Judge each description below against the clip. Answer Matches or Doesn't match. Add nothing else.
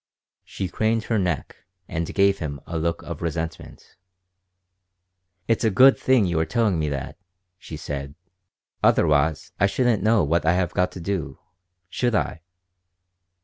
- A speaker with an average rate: Matches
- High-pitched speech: Doesn't match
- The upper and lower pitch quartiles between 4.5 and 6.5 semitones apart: Matches